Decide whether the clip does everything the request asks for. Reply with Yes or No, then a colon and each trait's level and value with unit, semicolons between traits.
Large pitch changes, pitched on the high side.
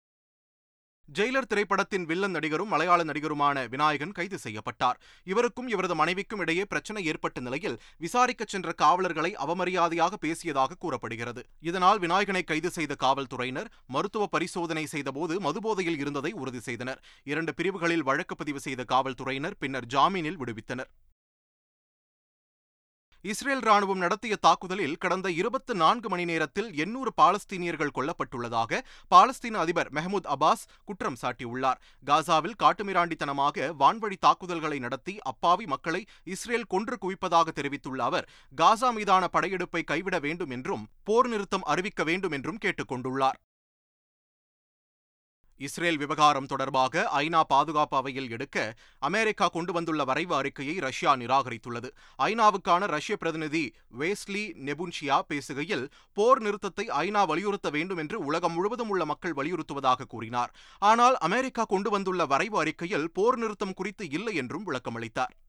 No: wide, 6.0 semitones; medium, 165 Hz